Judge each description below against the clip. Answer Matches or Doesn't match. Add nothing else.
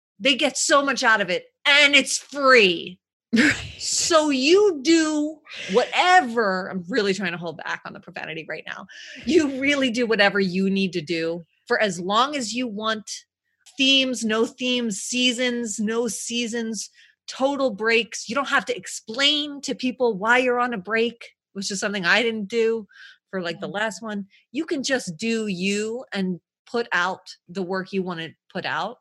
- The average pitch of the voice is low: Doesn't match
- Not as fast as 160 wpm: Doesn't match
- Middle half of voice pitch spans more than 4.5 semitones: Matches